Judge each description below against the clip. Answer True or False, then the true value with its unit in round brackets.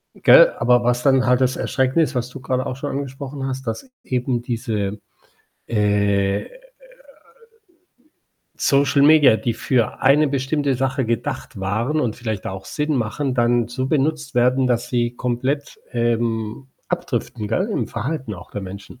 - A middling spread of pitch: True (3.1 semitones)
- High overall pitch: False (125 Hz)